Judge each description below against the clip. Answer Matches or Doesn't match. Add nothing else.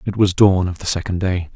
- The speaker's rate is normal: Doesn't match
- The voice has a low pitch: Matches